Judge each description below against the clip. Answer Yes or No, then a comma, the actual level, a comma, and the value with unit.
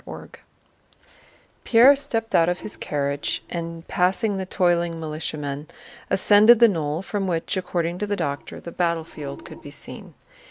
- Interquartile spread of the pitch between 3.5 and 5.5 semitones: Yes, average, 4.2 semitones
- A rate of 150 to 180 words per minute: Yes, average, 155 wpm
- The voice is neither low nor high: Yes, medium, 175 Hz